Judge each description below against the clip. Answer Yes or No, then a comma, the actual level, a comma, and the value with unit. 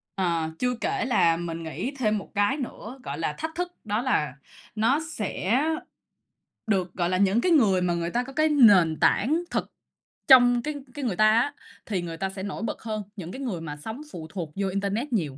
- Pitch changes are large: Yes, wide, 6.1 semitones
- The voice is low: No, high, 210 Hz